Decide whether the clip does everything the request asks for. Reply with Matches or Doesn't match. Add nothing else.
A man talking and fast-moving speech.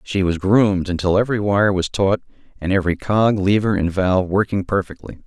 Doesn't match